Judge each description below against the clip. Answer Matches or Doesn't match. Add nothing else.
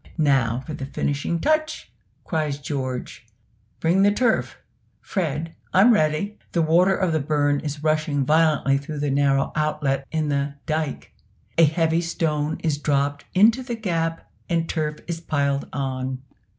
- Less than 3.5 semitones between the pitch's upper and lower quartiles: Matches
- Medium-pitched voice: Matches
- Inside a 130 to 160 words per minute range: Matches